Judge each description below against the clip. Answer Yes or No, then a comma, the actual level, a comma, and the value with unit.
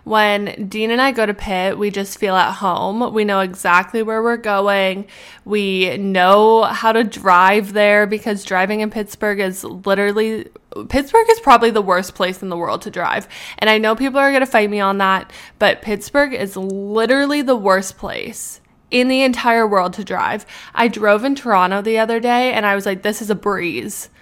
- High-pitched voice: Yes, high, 210 Hz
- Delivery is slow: No, average, 200 wpm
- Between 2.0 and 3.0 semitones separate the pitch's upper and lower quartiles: Yes, narrow, 2.6 semitones